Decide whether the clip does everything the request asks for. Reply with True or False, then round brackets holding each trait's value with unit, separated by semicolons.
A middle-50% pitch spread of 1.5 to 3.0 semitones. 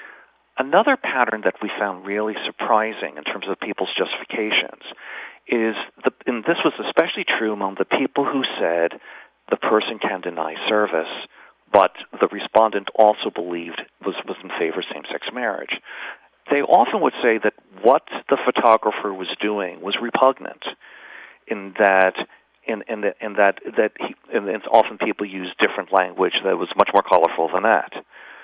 True (2.6 semitones)